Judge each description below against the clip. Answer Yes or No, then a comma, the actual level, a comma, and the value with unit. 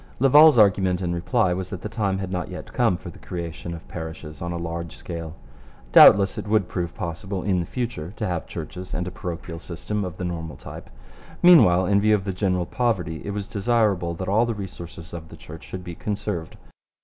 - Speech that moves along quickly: Yes, fast, 210 wpm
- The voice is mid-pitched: No, very low, 90 Hz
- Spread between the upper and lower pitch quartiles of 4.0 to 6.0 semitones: No, average, 3.2 semitones